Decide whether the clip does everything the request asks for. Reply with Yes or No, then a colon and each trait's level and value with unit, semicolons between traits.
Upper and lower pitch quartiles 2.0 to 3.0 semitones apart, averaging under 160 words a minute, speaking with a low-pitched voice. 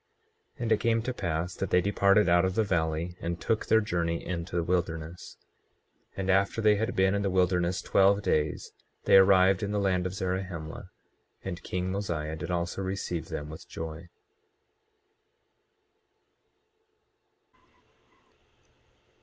Yes: narrow, 2.5 semitones; average, 145 wpm; very low, 90 Hz